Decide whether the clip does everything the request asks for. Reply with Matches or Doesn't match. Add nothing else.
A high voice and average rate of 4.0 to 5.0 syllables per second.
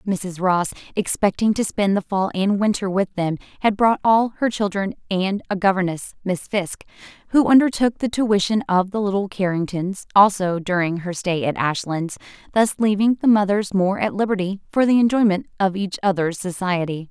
Matches